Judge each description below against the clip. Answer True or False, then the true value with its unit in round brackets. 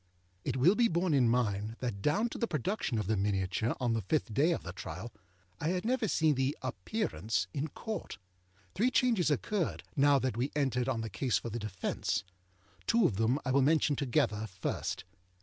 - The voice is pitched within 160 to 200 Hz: False (130 Hz)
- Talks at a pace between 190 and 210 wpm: True (195 wpm)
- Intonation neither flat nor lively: False (6.6 semitones)